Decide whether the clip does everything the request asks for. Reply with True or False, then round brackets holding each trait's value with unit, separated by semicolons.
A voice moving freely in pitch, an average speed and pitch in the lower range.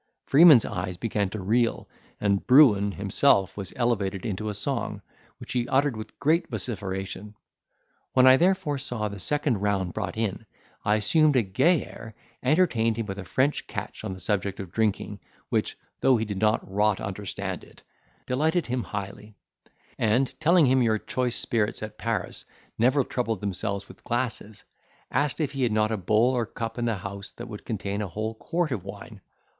False (4.2 semitones; 175 wpm; 110 Hz)